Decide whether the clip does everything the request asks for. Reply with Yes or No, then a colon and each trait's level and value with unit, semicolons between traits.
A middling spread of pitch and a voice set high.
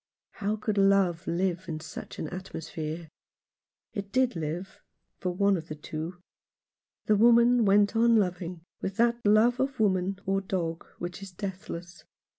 Yes: average, 3.4 semitones; high, 195 Hz